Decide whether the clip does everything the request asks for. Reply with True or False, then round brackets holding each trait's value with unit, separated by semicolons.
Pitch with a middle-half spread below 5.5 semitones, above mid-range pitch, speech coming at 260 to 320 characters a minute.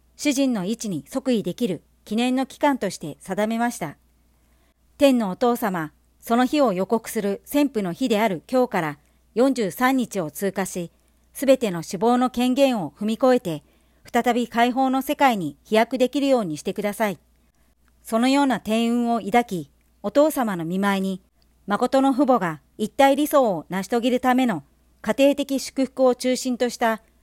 True (5.1 semitones; 230 Hz; 300 characters per minute)